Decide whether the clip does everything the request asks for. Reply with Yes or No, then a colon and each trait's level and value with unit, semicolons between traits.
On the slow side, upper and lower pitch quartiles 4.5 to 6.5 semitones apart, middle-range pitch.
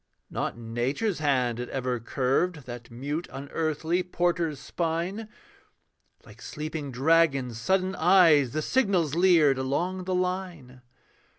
Yes: slow, 115 wpm; average, 5.3 semitones; medium, 155 Hz